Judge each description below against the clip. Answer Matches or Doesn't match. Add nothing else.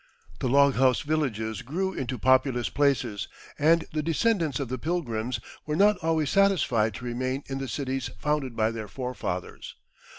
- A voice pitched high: Doesn't match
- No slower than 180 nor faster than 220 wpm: Doesn't match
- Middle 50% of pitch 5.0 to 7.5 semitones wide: Doesn't match